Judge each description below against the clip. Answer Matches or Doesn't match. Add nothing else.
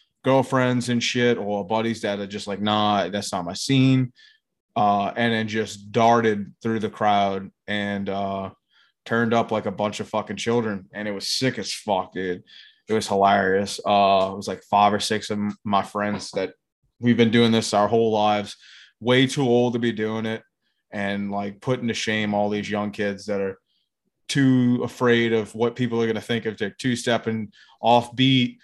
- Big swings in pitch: Doesn't match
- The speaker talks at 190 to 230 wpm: Matches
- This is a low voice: Matches